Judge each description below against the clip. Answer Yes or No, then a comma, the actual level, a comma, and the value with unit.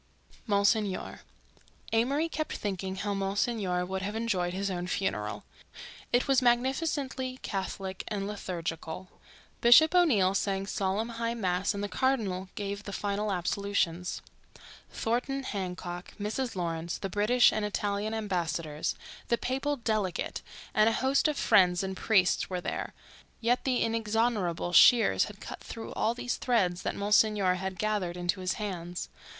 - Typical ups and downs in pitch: Yes, average, 4.0 semitones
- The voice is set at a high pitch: Yes, high, 200 Hz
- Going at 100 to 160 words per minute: Yes, average, 140 wpm